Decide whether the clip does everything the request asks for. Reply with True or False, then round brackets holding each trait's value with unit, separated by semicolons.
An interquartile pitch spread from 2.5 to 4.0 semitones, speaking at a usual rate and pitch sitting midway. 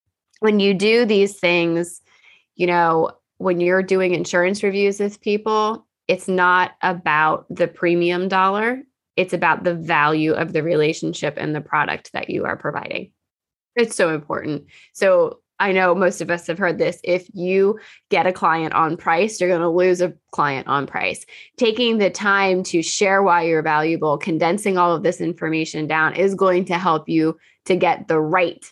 True (2.8 semitones; 175 wpm; 180 Hz)